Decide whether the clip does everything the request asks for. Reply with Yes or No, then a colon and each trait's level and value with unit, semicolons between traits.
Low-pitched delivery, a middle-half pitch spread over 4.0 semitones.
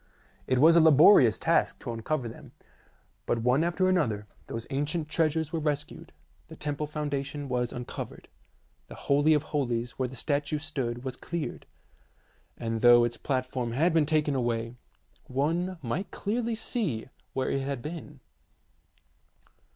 No: medium, 145 Hz; average, 4.4 semitones